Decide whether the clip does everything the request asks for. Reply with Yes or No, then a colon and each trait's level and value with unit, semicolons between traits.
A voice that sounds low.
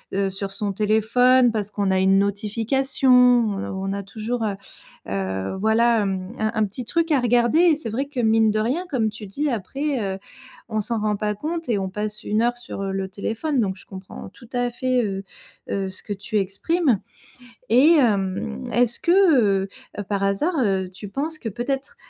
No: high, 220 Hz